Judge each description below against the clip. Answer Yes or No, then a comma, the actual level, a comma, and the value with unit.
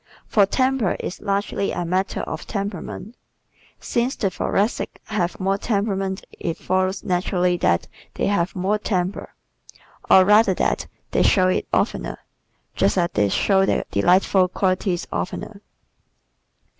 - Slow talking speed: Yes, slow, 130 wpm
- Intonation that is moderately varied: No, narrow, 2.0 semitones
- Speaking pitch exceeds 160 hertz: Yes, high, 190 Hz